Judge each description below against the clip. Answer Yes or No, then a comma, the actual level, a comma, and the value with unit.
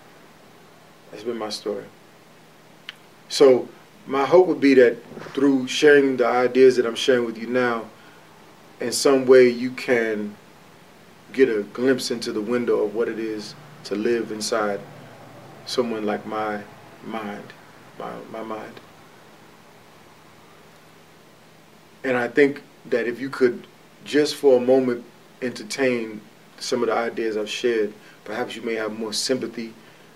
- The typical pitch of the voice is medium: No, low, 120 Hz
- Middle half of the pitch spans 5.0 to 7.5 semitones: No, average, 3.0 semitones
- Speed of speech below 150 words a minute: Yes, slow, 135 wpm